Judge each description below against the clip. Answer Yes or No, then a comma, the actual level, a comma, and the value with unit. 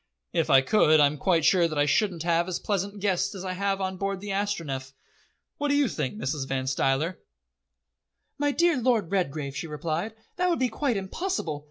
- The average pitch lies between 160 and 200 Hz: Yes, medium, 185 Hz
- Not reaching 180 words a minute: No, average, 200 wpm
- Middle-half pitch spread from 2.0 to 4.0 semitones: No, wide, 5.5 semitones